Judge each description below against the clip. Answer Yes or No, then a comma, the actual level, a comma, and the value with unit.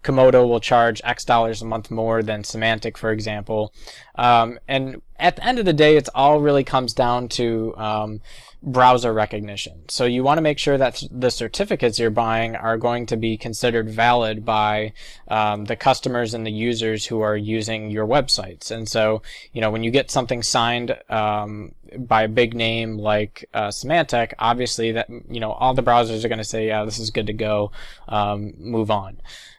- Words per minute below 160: No, average, 195 wpm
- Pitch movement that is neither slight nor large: No, narrow, 2.2 semitones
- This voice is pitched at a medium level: No, low, 115 Hz